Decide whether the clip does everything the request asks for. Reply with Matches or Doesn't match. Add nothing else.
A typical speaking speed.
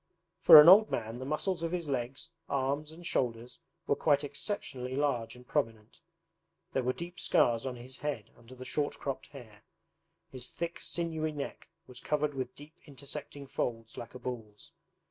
Matches